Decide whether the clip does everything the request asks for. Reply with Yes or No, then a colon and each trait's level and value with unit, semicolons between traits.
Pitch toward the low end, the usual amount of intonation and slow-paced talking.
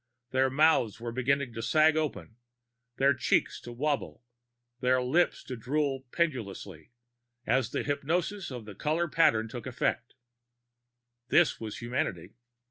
Yes: low, 130 Hz; average, 4.5 semitones; slow, 130 wpm